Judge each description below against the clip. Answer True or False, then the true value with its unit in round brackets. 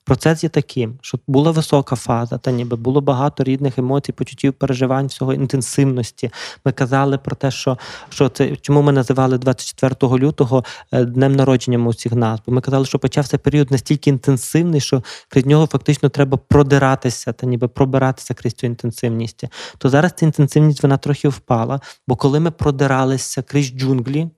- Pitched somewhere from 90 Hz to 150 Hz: True (135 Hz)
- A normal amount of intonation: False (2.0 semitones)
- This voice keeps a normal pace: False (160 wpm)